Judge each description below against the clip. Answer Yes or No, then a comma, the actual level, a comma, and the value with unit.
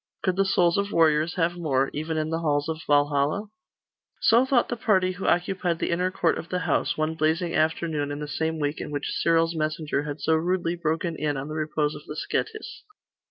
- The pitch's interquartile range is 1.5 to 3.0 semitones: Yes, average, 2.7 semitones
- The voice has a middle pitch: Yes, medium, 160 Hz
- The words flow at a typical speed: No, fast, 210 wpm